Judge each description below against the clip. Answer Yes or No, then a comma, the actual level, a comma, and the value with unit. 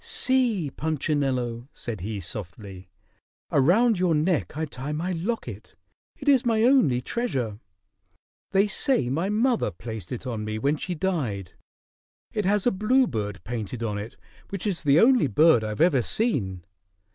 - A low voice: No, medium, 150 Hz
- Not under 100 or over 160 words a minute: Yes, average, 150 wpm